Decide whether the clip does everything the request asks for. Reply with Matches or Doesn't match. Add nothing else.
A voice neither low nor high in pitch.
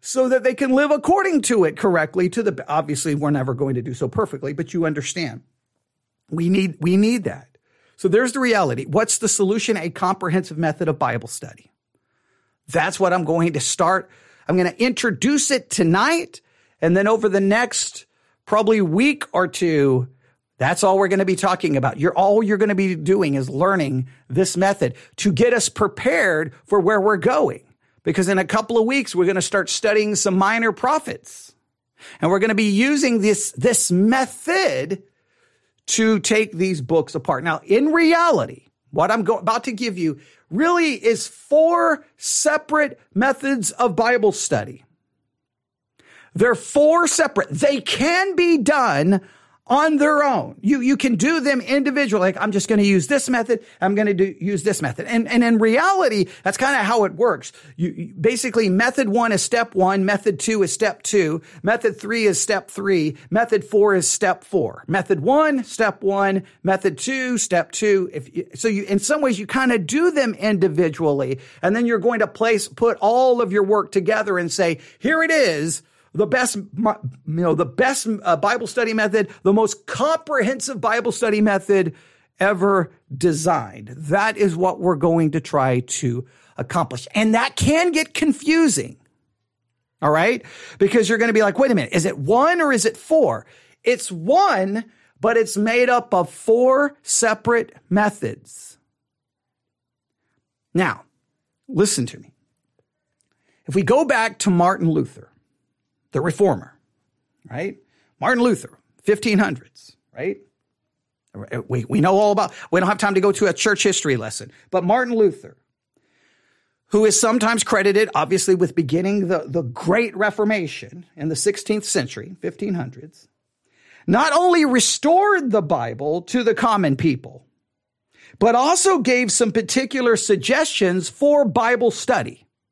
Doesn't match